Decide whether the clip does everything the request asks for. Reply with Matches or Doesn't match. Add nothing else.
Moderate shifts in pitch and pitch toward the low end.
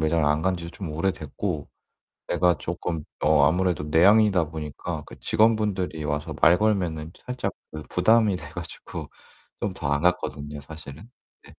Matches